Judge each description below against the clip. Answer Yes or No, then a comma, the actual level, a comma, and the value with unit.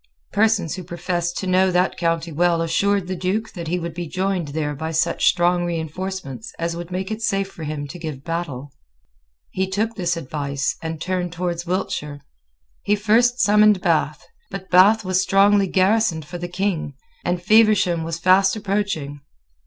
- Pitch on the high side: No, medium, 180 Hz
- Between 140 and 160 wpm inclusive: No, average, 170 wpm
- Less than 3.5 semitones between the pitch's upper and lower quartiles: Yes, average, 2.9 semitones